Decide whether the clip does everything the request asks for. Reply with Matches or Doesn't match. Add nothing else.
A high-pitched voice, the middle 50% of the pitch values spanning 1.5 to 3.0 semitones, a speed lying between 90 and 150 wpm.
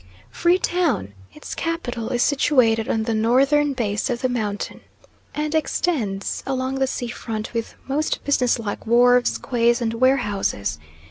Doesn't match